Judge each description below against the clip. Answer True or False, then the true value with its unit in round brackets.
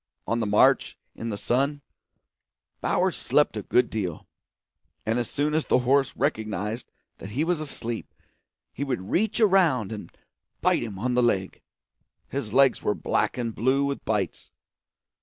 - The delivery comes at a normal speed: True (160 wpm)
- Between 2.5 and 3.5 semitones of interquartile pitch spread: False (4.6 semitones)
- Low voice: True (120 Hz)